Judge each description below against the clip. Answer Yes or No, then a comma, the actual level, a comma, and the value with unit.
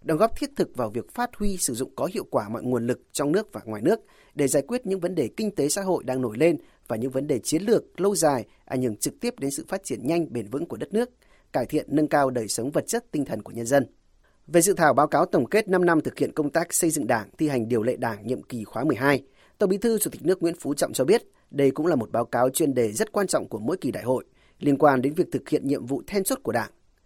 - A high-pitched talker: No, medium, 150 Hz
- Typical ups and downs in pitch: No, wide, 6.4 semitones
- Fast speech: Yes, fast, 295 wpm